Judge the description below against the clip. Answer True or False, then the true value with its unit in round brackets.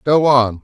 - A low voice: True (130 Hz)